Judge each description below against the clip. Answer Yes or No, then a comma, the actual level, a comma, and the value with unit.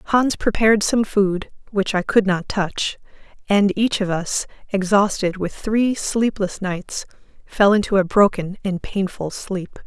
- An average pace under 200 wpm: Yes, average, 150 wpm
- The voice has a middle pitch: No, high, 200 Hz